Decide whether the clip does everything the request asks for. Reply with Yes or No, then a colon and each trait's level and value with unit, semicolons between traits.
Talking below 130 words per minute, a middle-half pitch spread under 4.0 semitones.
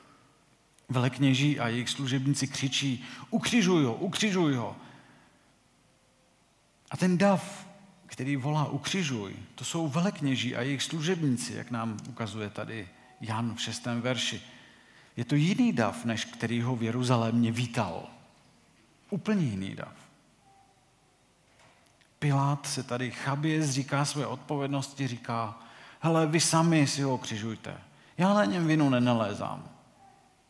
No: average, 120 wpm; average, 4.3 semitones